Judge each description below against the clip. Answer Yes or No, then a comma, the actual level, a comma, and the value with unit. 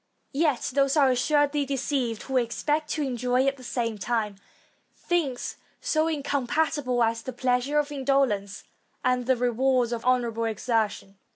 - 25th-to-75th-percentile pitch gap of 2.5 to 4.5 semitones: Yes, average, 3.2 semitones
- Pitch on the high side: Yes, very high, 255 Hz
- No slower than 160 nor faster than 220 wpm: No, average, 145 wpm